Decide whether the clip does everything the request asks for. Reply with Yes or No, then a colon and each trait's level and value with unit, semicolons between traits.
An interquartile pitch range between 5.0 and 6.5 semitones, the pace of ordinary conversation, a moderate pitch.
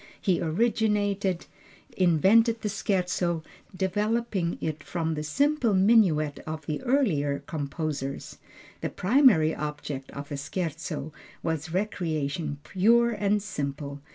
No: wide, 5.5 semitones; slow, 110 wpm; medium, 175 Hz